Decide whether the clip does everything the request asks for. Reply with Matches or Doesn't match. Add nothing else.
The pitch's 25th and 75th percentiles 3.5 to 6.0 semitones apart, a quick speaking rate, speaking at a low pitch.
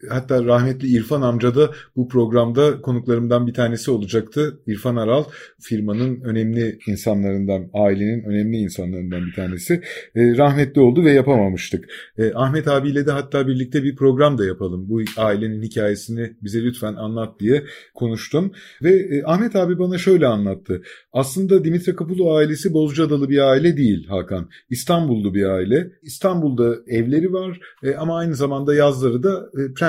Matches